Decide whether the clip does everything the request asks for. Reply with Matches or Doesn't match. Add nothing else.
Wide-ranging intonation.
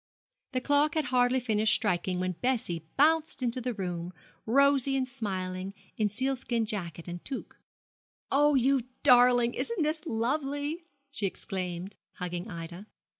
Matches